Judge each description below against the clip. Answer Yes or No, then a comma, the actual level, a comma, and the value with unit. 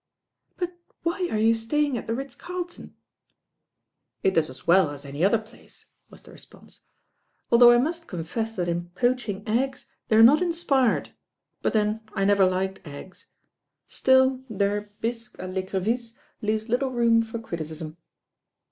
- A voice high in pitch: Yes, high, 225 Hz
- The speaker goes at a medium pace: Yes, average, 160 wpm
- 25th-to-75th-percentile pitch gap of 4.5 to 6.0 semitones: Yes, average, 4.9 semitones